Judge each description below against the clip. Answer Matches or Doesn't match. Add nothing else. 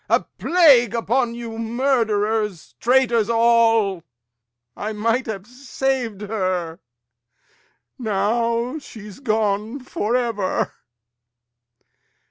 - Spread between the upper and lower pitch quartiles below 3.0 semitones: Matches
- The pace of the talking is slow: Matches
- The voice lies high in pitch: Matches